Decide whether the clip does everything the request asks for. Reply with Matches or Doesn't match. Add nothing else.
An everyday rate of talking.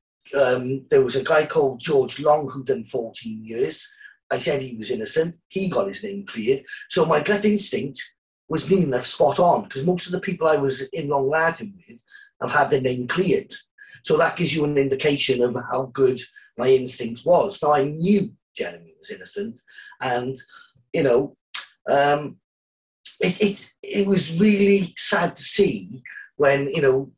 Matches